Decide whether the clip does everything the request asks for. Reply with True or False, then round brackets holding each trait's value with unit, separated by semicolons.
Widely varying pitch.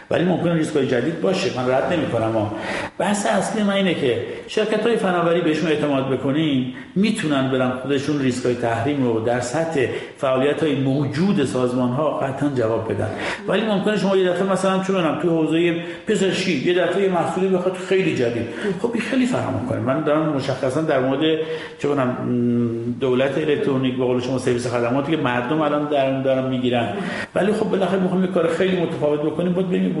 True (5.7 semitones)